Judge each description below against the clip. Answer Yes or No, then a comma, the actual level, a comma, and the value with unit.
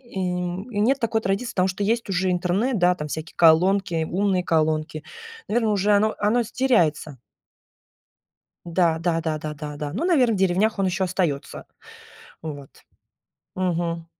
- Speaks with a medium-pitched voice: Yes, medium, 180 Hz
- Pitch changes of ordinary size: Yes, average, 4.1 semitones